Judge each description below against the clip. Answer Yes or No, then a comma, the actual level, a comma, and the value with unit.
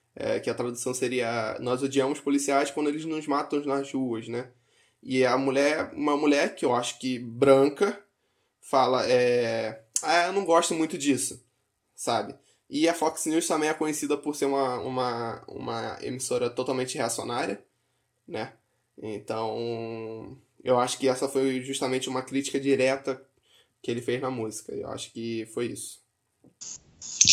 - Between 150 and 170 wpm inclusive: Yes, average, 155 wpm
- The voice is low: Yes, low, 130 Hz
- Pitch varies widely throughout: No, average, 2.7 semitones